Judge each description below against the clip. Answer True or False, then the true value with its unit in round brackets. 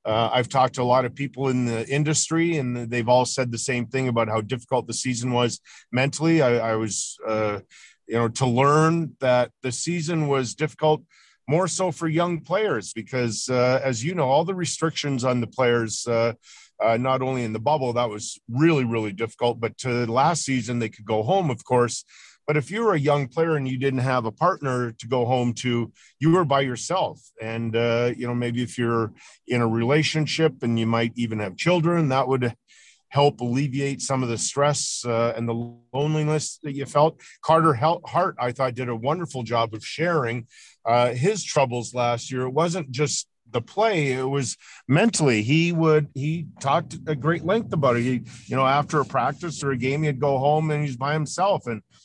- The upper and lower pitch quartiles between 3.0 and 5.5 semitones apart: True (4.2 semitones)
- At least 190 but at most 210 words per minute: True (205 wpm)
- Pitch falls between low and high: False (130 Hz)